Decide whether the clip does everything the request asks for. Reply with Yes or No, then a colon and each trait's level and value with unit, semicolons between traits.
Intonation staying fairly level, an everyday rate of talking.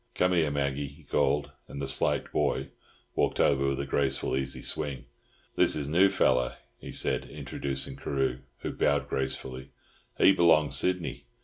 Yes: narrow, 2.1 semitones; average, 155 wpm